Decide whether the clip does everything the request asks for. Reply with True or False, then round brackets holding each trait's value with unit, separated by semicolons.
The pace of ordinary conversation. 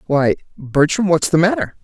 True (165 wpm)